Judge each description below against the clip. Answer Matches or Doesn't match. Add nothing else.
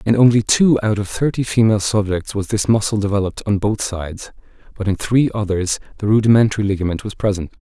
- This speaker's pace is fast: Doesn't match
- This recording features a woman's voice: Doesn't match